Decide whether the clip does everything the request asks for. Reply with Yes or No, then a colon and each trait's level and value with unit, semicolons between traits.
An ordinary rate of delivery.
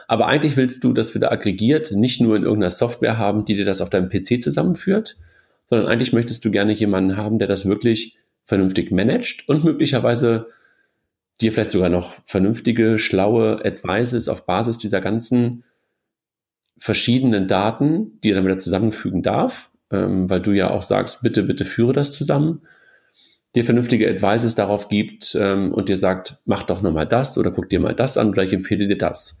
Yes: average, 175 wpm